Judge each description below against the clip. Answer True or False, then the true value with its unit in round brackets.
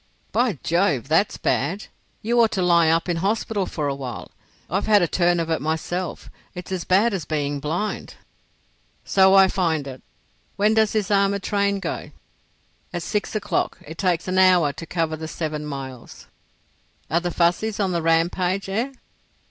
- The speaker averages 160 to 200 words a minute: True (170 wpm)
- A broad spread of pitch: False (3.8 semitones)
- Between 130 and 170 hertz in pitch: False (180 Hz)